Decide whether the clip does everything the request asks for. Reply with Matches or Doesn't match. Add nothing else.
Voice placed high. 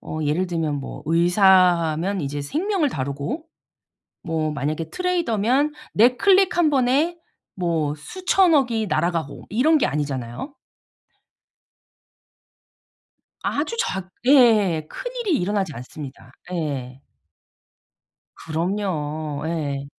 Doesn't match